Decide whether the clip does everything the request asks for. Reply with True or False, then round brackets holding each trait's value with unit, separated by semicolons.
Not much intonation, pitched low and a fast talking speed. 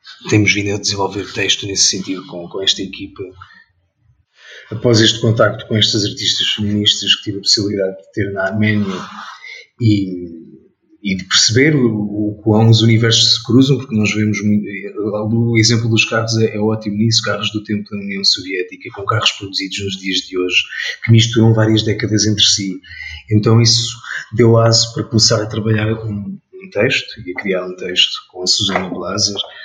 True (2.3 semitones; 105 Hz; 190 wpm)